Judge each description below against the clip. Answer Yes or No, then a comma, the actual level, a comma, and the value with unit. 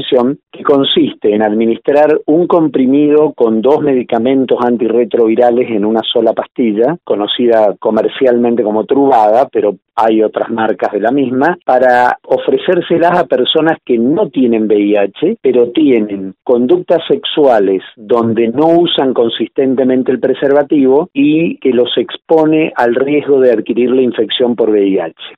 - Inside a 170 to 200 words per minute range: No, average, 130 wpm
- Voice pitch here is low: Yes, low, 125 Hz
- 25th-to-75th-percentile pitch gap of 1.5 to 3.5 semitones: No, average, 4.6 semitones